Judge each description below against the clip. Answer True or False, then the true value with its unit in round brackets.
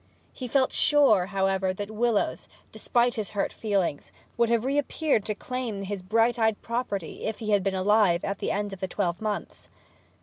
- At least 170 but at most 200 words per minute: True (190 wpm)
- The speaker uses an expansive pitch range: False (3.3 semitones)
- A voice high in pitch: True (210 Hz)